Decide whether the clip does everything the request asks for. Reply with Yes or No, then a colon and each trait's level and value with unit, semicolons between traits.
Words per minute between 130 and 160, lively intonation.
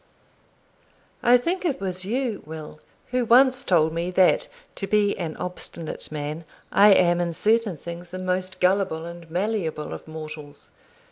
No: average, 150 wpm; average, 4.4 semitones